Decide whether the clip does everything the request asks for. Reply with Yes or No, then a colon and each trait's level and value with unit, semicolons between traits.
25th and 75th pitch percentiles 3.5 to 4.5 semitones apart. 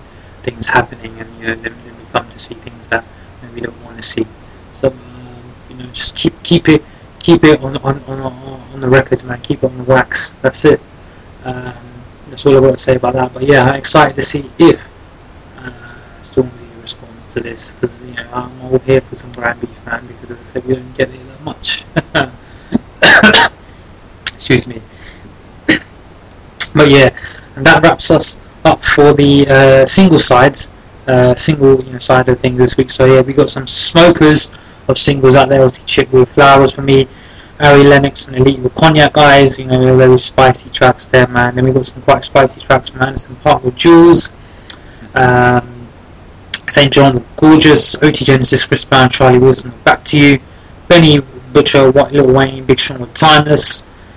No: average, 2.7 semitones